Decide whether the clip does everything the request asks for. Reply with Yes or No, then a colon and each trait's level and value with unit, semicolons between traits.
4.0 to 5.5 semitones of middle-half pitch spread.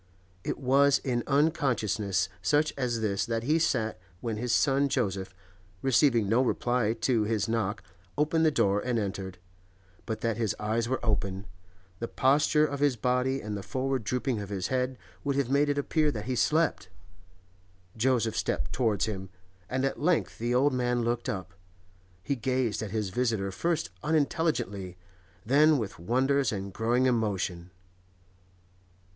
Yes: average, 4.5 semitones